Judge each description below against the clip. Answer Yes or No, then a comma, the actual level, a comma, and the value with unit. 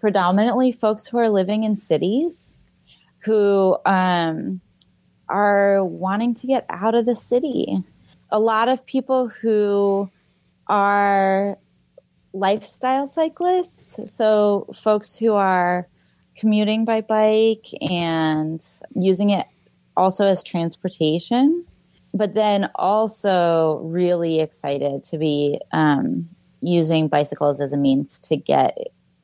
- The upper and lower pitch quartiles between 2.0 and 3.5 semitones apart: No, average, 4.7 semitones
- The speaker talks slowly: Yes, slow, 110 wpm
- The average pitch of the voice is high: Yes, high, 200 Hz